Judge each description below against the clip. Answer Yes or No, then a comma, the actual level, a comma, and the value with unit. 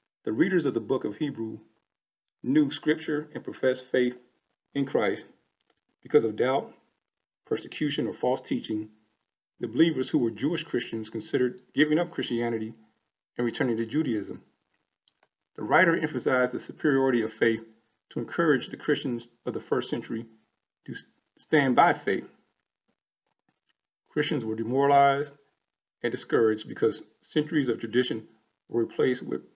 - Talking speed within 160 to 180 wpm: No, slow, 135 wpm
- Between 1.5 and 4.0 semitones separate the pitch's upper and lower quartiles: No, average, 4.4 semitones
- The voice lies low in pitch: Yes, low, 125 Hz